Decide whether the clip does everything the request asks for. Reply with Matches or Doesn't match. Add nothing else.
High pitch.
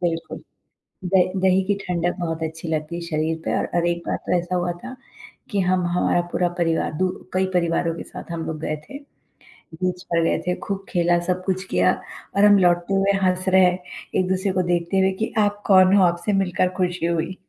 Doesn't match